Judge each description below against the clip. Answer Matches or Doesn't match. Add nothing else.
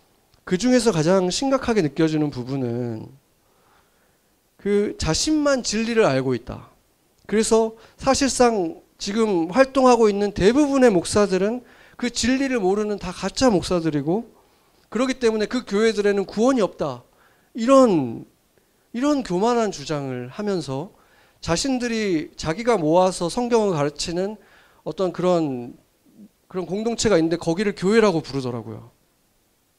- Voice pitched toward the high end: Matches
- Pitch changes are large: Matches